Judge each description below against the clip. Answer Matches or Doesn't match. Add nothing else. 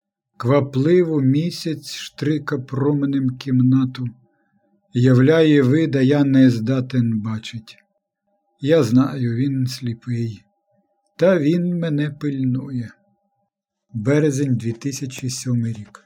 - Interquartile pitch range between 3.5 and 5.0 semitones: Matches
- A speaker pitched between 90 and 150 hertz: Matches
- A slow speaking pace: Matches